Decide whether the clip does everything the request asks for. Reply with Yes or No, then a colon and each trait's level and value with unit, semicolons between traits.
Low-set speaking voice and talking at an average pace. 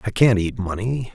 No: low, 105 Hz; fast, 210 wpm